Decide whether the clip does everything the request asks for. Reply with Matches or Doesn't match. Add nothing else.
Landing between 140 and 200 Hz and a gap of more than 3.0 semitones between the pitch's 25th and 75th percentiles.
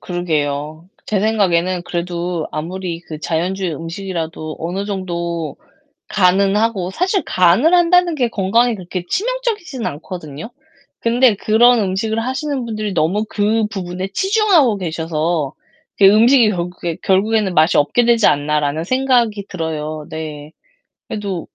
Matches